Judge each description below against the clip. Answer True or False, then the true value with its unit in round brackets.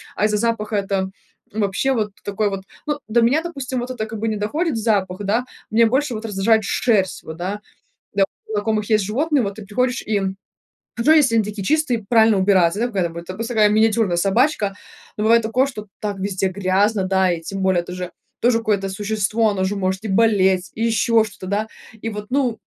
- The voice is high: True (215 Hz)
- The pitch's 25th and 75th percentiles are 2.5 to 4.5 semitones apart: True (2.9 semitones)